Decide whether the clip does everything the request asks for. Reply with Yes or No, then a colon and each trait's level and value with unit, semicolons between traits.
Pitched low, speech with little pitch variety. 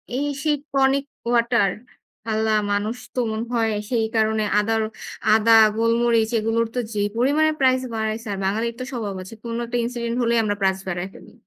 No: high, 230 Hz; narrow, 1.8 semitones